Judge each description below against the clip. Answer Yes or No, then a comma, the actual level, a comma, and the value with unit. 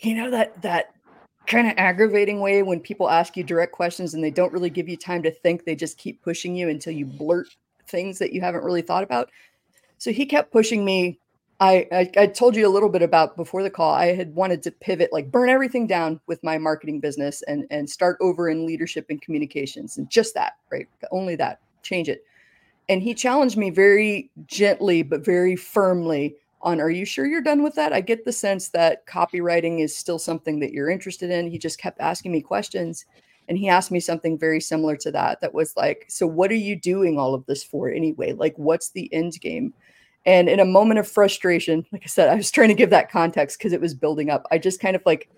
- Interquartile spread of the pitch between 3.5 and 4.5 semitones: Yes, average, 4.0 semitones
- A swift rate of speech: Yes, fast, 230 wpm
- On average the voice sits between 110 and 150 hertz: No, medium, 180 Hz